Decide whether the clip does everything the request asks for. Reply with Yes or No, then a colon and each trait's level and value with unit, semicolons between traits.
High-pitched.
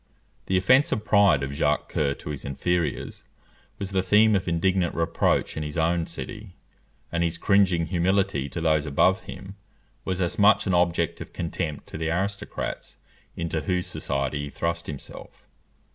No: very low, 85 Hz